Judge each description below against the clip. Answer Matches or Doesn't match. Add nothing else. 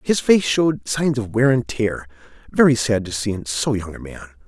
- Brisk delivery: Matches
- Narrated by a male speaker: Matches